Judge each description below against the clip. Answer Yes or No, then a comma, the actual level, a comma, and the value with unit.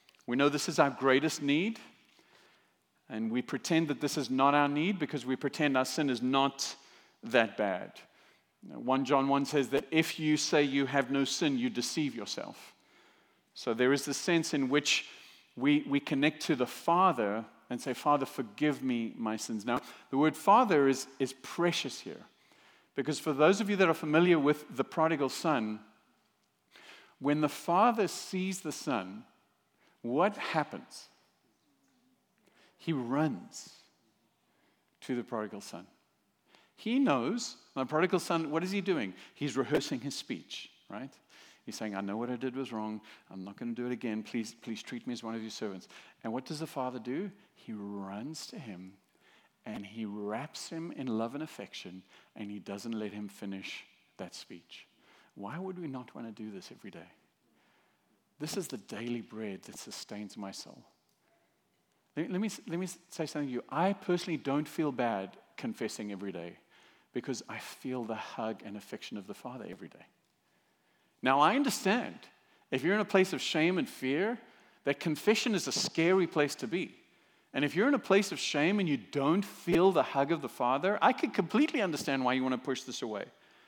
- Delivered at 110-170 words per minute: No, average, 185 wpm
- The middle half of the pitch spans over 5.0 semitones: Yes, wide, 5.5 semitones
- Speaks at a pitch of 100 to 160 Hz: Yes, medium, 140 Hz